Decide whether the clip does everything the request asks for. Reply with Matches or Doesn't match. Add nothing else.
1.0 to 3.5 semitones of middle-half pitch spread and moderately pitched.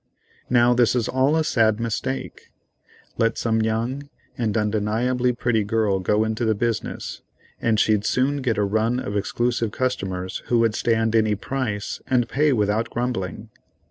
Doesn't match